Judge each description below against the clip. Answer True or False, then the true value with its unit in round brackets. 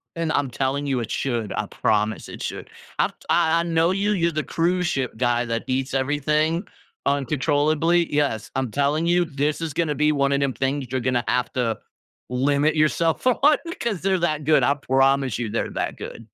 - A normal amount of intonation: True (4.0 semitones)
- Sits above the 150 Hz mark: False (145 Hz)